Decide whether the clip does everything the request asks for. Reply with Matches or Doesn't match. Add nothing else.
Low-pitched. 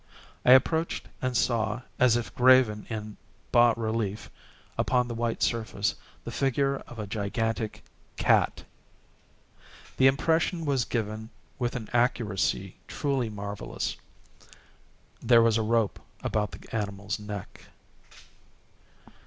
Matches